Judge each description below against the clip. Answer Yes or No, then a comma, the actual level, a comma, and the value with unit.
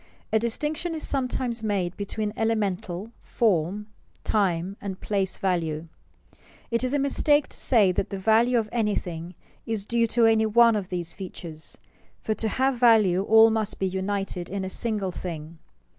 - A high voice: Yes, high, 210 Hz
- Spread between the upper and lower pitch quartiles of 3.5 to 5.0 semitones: Yes, average, 3.8 semitones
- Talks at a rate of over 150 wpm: Yes, average, 165 wpm